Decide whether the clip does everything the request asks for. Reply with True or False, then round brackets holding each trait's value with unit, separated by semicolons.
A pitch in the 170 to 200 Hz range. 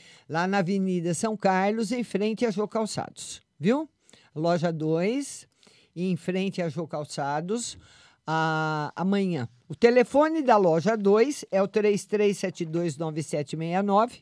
True (190 Hz)